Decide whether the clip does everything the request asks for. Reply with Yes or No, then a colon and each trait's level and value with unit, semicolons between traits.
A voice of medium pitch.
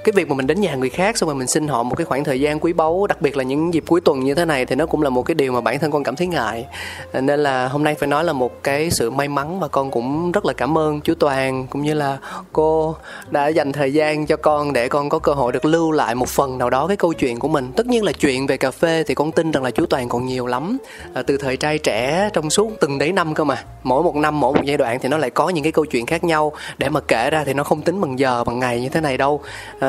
Yes: medium, 150 Hz